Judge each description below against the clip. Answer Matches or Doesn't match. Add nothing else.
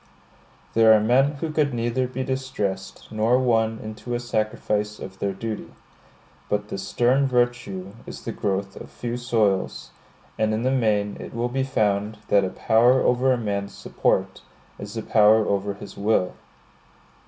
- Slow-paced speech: Doesn't match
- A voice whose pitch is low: Matches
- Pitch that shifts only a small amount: Doesn't match